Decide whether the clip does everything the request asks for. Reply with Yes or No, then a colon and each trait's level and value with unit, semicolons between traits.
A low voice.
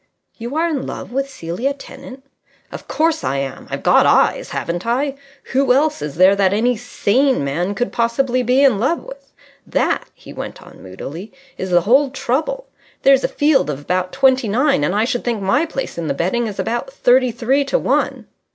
No: high, 245 Hz